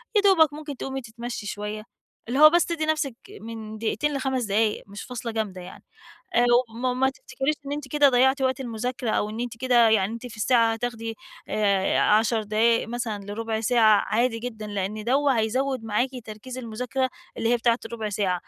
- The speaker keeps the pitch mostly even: No, average, 3.2 semitones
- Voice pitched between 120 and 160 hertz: No, high, 235 Hz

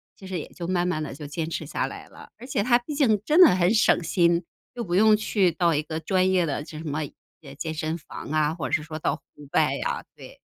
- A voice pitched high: No, medium, 170 Hz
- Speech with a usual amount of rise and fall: Yes, average, 4.4 semitones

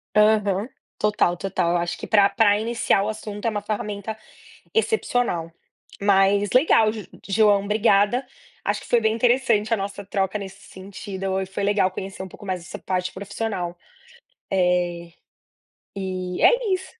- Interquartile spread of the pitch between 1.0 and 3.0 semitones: Yes, narrow, 2.4 semitones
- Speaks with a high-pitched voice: Yes, high, 200 Hz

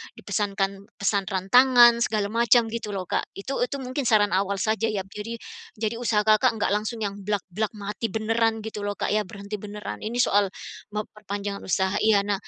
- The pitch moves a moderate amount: No, narrow, 2.0 semitones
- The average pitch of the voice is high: Yes, high, 210 Hz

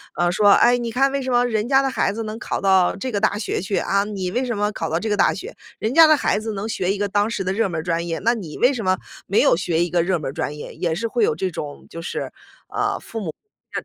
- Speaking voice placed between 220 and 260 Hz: No, high, 205 Hz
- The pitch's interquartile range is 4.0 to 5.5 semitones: Yes, average, 4.6 semitones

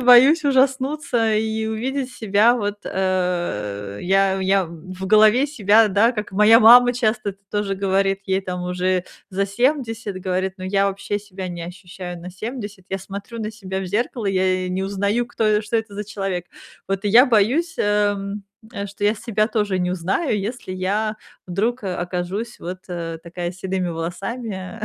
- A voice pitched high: Yes, high, 200 Hz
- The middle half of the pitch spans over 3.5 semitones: No, average, 3.1 semitones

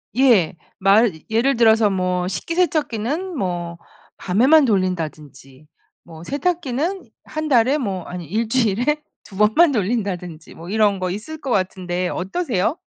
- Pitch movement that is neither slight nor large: No, wide, 7.0 semitones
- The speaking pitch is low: No, high, 215 Hz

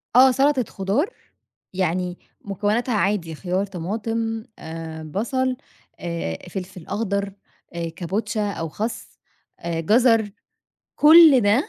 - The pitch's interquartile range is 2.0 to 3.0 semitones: No, average, 4.6 semitones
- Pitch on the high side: Yes, high, 205 Hz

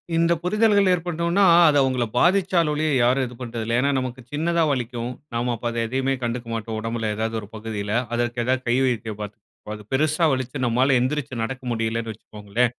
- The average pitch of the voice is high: No, low, 125 Hz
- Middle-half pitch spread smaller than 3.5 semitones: No, average, 4.3 semitones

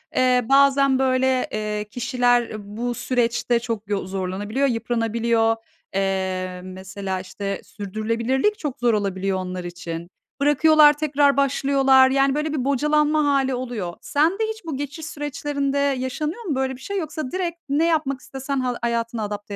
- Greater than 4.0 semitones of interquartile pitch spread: Yes, average, 5.1 semitones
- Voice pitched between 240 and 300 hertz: Yes, very high, 255 Hz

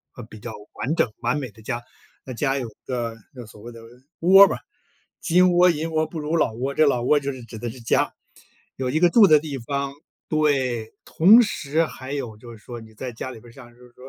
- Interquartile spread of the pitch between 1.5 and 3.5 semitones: No, average, 4.6 semitones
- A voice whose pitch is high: No, low, 130 Hz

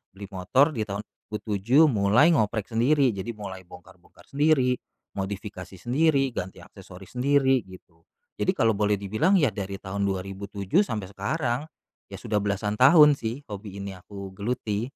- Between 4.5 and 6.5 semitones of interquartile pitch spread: Yes, average, 5.0 semitones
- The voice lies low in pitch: Yes, low, 105 Hz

